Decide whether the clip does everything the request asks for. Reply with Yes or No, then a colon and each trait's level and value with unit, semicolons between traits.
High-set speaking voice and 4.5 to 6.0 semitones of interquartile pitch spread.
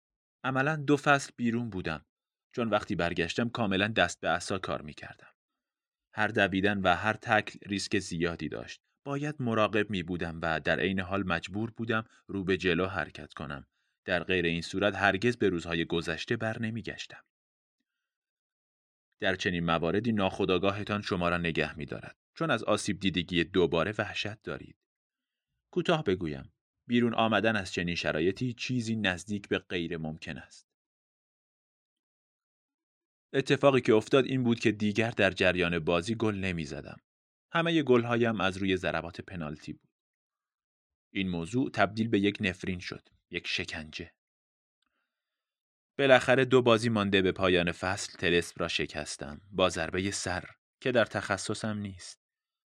No: low, 100 Hz; average, 4.9 semitones